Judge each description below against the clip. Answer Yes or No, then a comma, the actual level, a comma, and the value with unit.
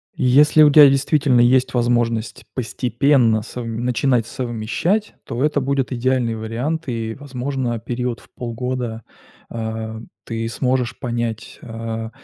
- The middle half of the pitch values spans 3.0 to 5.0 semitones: No, narrow, 2.6 semitones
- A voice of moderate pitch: No, low, 120 Hz